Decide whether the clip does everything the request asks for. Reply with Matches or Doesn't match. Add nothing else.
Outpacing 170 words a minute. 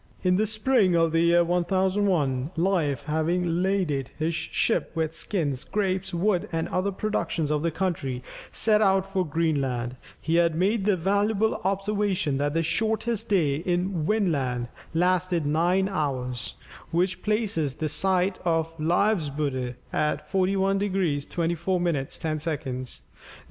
Doesn't match